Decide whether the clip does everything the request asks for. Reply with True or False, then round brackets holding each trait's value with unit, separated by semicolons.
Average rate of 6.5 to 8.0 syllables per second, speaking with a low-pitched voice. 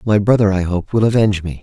True (6.6 syllables/s; 100 Hz)